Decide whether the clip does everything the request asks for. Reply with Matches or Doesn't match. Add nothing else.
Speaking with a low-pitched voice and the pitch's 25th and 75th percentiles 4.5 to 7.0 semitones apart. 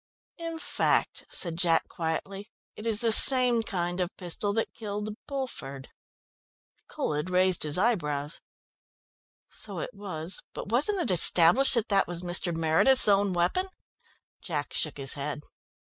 Doesn't match